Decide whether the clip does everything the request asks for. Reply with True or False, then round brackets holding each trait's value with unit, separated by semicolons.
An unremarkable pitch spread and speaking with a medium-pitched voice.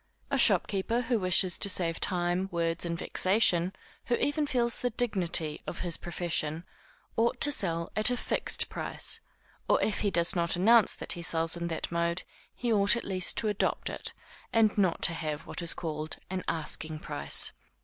True (4.3 semitones; 180 Hz)